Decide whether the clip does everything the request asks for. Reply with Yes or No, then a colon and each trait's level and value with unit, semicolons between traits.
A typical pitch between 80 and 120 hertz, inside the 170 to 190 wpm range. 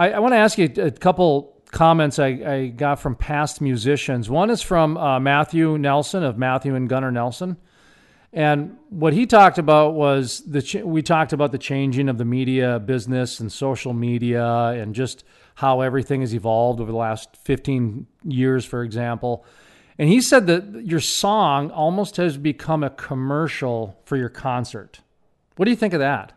No: medium, 140 Hz; average, 175 wpm